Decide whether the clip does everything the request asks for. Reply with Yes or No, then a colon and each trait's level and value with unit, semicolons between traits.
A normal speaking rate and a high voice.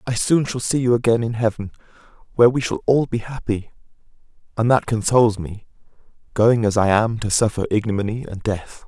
No: average, 185 wpm; low, 115 Hz